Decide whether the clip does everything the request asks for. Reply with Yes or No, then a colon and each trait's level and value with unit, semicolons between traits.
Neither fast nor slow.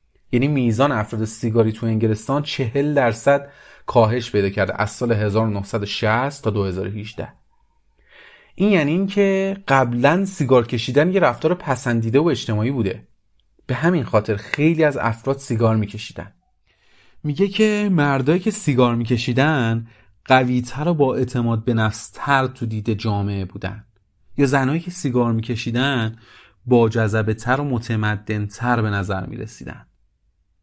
No: slow, 130 wpm